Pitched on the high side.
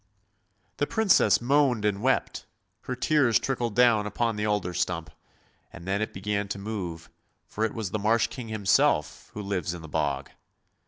No: low, 105 Hz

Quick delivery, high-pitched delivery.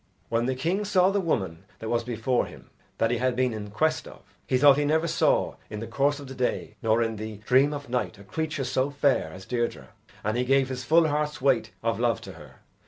No: fast, 240 wpm; low, 130 Hz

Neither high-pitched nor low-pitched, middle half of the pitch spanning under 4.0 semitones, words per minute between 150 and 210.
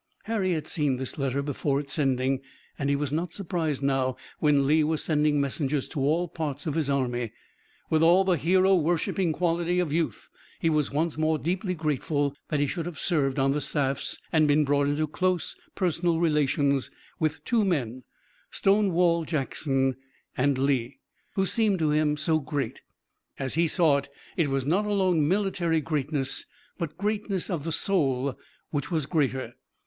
Yes: medium, 155 Hz; average, 3.6 semitones; average, 170 wpm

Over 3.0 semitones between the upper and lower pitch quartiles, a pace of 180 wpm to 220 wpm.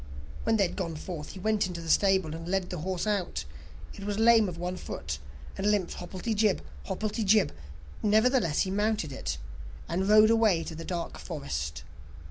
Yes: average, 4.1 semitones; average, 185 wpm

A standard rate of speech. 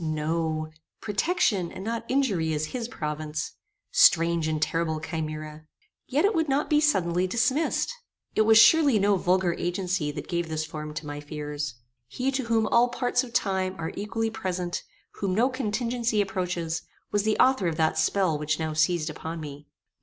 Yes: average, 170 wpm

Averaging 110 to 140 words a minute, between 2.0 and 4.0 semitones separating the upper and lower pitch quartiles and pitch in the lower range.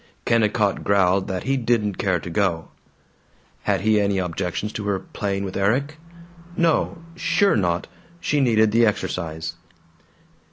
Yes: slow, 135 wpm; average, 3.7 semitones; low, 100 Hz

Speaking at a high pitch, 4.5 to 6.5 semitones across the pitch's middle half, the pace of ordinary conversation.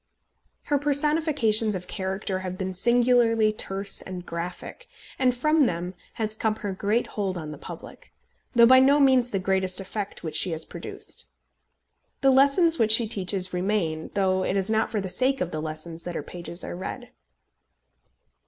Yes: high, 200 Hz; average, 5.0 semitones; average, 170 wpm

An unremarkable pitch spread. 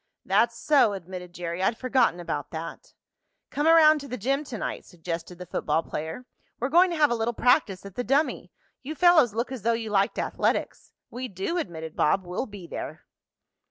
No: wide, 7.1 semitones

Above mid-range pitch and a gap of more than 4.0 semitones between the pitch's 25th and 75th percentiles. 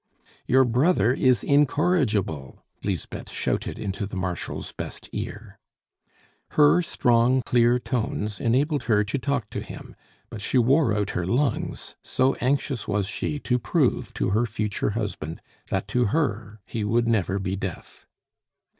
No: low, 115 Hz; average, 4.4 semitones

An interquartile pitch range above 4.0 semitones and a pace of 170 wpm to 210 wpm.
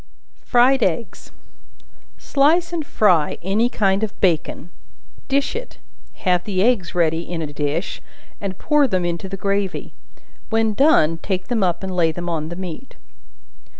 No: average, 5.2 semitones; average, 150 wpm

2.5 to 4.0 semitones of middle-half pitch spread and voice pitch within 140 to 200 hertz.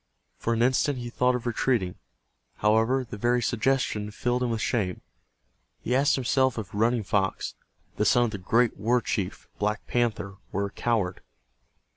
No: average, 2.9 semitones; low, 115 Hz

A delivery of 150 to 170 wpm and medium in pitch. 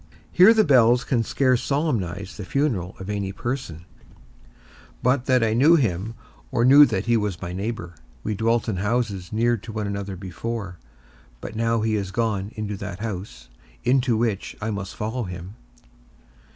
No: average, 165 wpm; low, 110 Hz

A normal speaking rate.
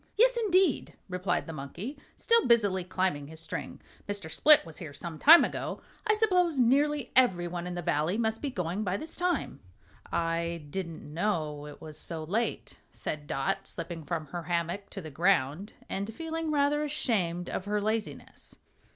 Yes: average, 170 wpm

